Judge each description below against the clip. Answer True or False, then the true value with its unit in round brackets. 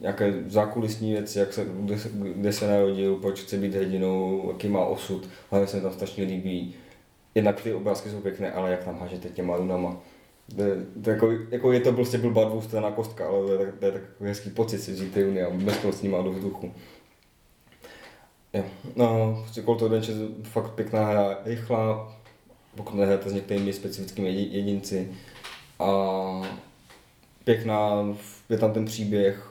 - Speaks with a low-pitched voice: True (100 Hz)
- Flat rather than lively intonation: True (2.1 semitones)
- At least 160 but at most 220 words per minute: True (170 wpm)